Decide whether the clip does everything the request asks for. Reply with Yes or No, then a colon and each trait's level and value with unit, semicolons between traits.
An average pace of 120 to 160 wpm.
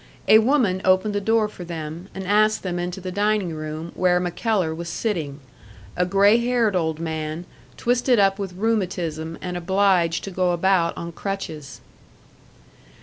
Yes: average, 155 wpm